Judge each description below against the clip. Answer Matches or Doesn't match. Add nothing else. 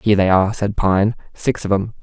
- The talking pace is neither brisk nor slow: Doesn't match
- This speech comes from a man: Matches